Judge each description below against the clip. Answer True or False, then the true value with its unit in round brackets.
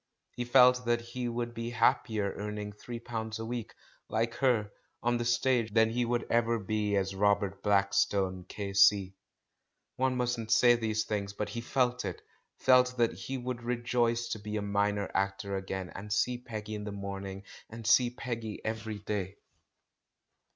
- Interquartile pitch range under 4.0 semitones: True (2.8 semitones)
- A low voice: True (110 Hz)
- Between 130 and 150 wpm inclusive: False (170 wpm)